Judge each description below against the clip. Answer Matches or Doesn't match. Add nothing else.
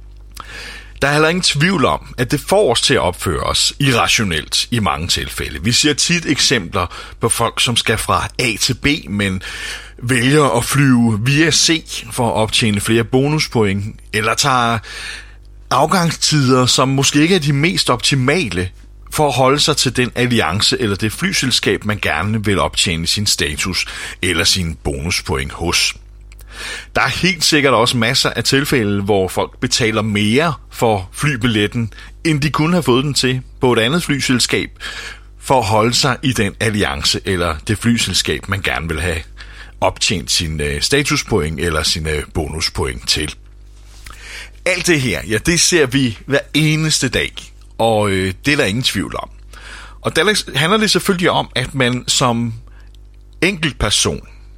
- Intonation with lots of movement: Matches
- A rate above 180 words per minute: Doesn't match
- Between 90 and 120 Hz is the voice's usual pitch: Matches